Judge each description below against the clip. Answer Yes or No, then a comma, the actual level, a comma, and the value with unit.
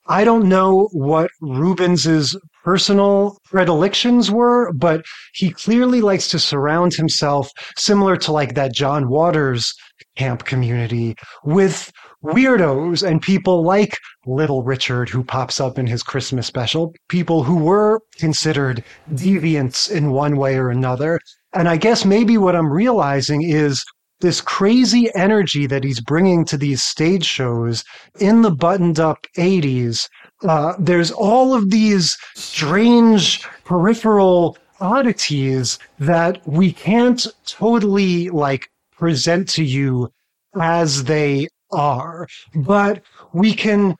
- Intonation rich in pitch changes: Yes, wide, 5.7 semitones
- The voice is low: No, medium, 170 Hz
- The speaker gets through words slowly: Yes, slow, 125 wpm